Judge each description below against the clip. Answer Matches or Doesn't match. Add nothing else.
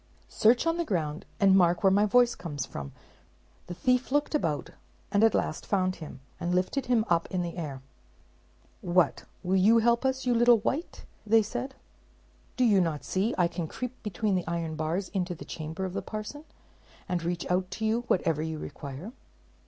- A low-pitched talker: Doesn't match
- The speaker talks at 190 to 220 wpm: Matches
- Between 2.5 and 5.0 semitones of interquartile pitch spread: Doesn't match